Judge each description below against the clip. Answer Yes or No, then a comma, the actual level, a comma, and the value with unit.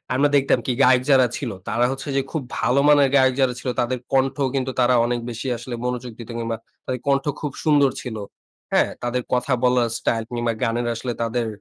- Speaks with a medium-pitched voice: No, low, 125 Hz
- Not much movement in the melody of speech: Yes, narrow, 2.0 semitones